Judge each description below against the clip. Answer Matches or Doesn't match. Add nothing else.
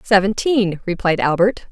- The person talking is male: Doesn't match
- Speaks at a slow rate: Matches